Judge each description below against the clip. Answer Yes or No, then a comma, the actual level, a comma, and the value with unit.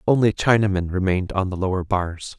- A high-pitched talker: No, very low, 95 Hz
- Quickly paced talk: No, average, 175 wpm